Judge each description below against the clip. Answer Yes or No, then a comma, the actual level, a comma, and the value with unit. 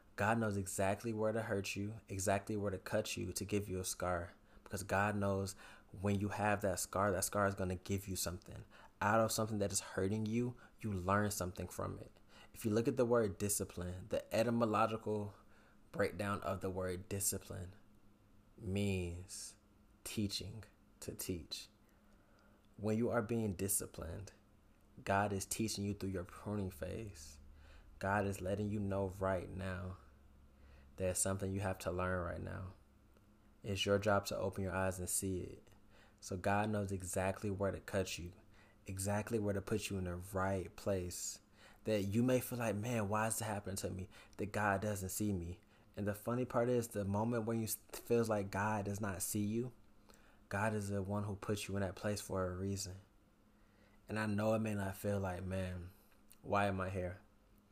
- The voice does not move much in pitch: Yes, narrow, 1.9 semitones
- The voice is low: Yes, low, 100 Hz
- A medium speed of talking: Yes, average, 185 wpm